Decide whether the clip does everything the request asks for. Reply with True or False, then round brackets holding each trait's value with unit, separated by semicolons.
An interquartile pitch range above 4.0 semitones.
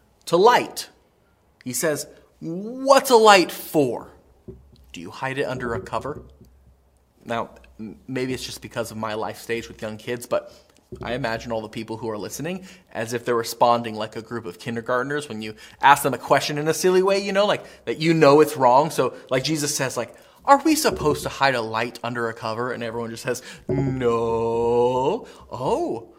True (4.6 semitones)